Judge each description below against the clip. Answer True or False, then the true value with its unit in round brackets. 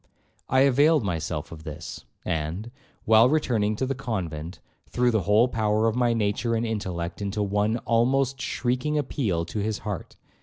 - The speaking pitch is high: False (110 Hz)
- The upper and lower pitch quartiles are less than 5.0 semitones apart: True (4.0 semitones)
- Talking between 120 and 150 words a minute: False (160 wpm)